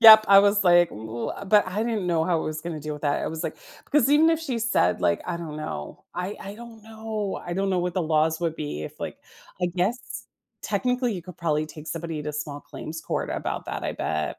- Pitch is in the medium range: Yes, medium, 175 Hz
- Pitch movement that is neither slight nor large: No, wide, 5.7 semitones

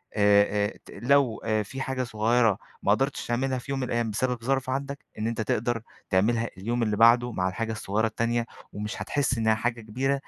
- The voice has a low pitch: Yes, low, 115 Hz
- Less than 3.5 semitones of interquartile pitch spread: Yes, average, 3.0 semitones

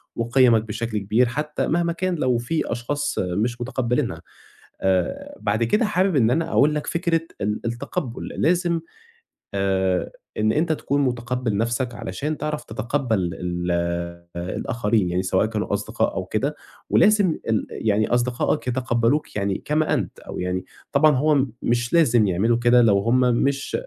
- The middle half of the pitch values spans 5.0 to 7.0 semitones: Yes, wide, 5.6 semitones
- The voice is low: Yes, low, 120 Hz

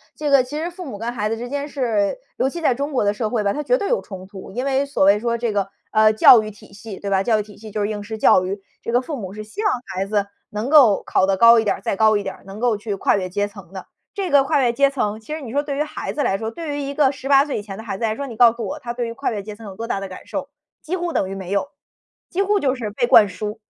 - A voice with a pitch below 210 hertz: No, high, 225 Hz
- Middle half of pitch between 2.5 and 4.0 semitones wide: No, average, 5.2 semitones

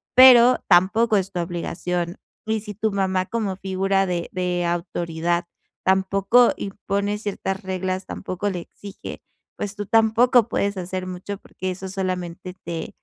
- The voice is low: No, high, 190 Hz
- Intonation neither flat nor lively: No, narrow, 2.3 semitones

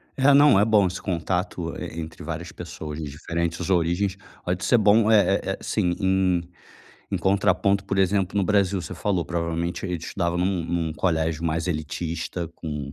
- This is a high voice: No, very low, 90 Hz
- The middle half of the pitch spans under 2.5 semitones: No, average, 2.9 semitones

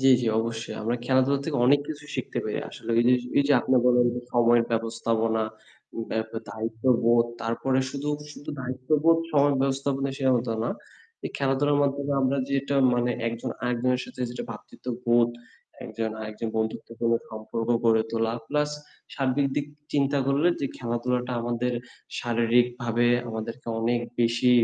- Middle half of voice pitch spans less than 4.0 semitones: Yes, average, 2.9 semitones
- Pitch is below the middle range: Yes, low, 125 Hz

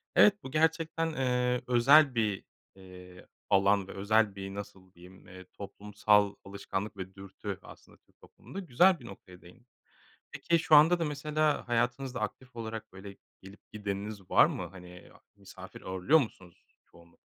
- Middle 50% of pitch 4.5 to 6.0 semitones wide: Yes, wide, 5.5 semitones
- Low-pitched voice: Yes, low, 105 Hz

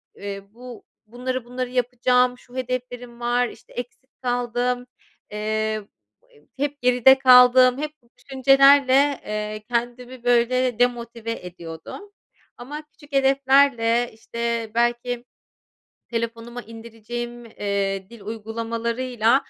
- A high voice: Yes, high, 245 Hz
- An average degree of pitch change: No, narrow, 1.7 semitones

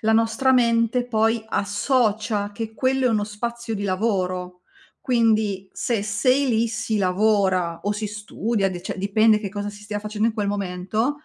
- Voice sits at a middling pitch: No, high, 215 Hz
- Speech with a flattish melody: Yes, narrow, 2.2 semitones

